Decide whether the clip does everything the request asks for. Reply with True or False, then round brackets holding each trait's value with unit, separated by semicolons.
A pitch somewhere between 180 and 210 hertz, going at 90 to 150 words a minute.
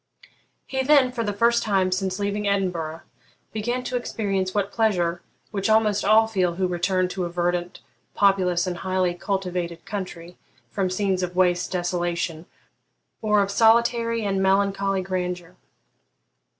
True (190 Hz; 140 wpm)